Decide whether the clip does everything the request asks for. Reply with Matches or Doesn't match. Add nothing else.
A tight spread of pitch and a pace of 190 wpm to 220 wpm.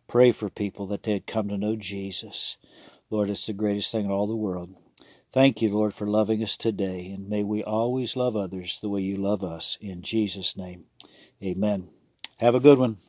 Matches